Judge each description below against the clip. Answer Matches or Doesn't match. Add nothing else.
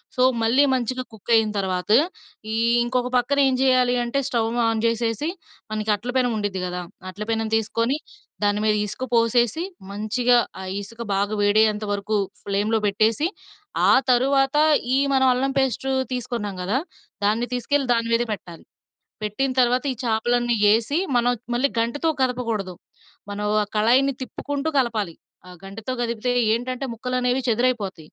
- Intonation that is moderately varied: Matches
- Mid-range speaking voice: Doesn't match